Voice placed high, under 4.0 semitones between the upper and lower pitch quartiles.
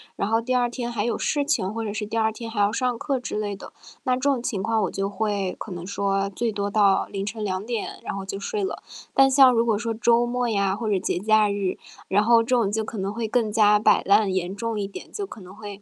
Yes: high, 215 Hz; average, 2.9 semitones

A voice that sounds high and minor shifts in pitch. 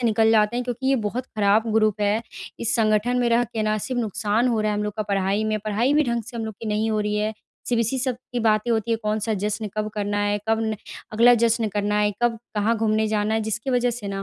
Yes: high, 220 Hz; narrow, 1.9 semitones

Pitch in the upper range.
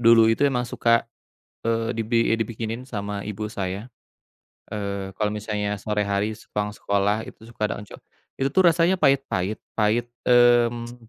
No: low, 110 Hz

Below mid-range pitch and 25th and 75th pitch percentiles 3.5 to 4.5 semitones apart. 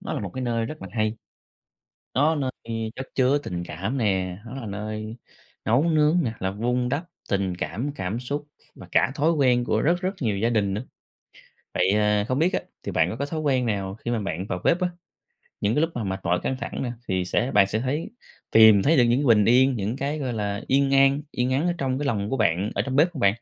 No: low, 120 Hz; average, 5.1 semitones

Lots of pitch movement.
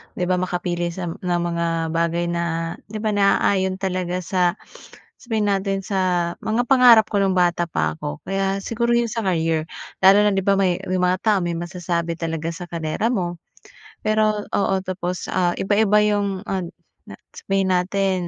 No: narrow, 2.6 semitones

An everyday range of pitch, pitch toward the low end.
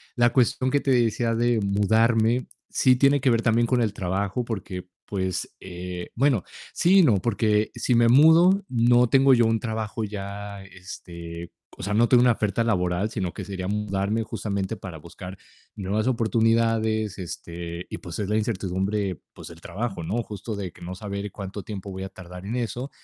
Yes: average, 3.6 semitones; low, 105 Hz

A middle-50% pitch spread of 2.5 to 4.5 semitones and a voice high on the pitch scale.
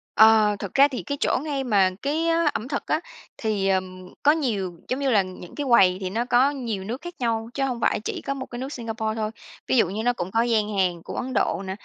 No: average, 5.3 semitones; high, 225 Hz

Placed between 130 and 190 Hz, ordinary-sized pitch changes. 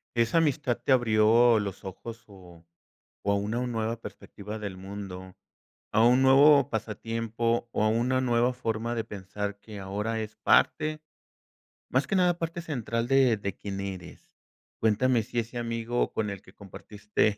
No: low, 115 Hz; average, 3.0 semitones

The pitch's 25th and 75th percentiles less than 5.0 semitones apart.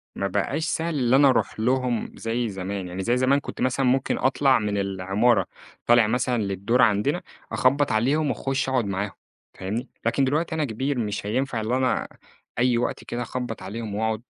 Yes: average, 4.0 semitones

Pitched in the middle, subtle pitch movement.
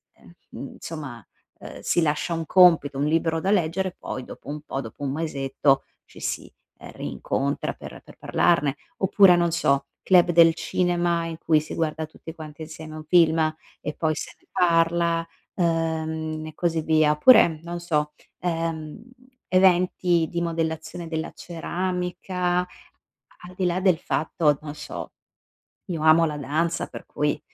Yes: medium, 165 Hz; narrow, 2.1 semitones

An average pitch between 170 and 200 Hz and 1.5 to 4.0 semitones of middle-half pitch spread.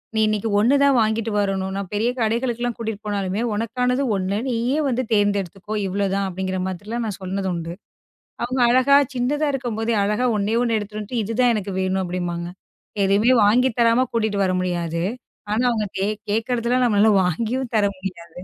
No: high, 215 Hz; average, 3.6 semitones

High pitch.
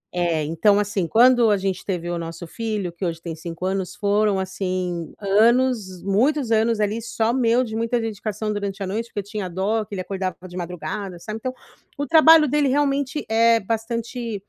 Yes: high, 210 Hz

